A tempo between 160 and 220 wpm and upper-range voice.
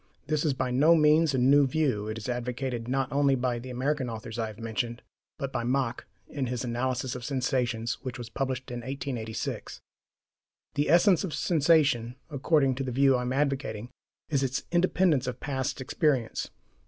No: average, 180 wpm; low, 130 Hz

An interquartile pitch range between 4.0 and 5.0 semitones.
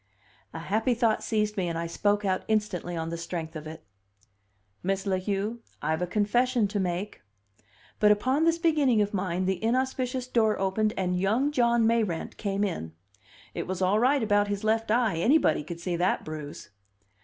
Yes: average, 4.3 semitones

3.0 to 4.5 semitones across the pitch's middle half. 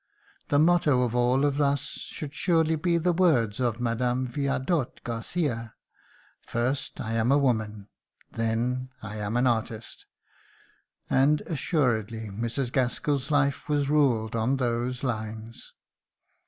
Yes: average, 3.9 semitones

